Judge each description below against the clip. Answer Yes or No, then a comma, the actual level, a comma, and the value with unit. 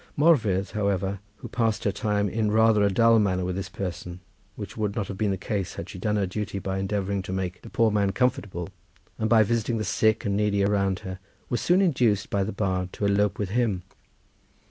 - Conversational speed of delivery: No, fast, 215 wpm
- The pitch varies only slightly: Yes, narrow, 2.3 semitones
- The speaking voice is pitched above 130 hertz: No, low, 100 Hz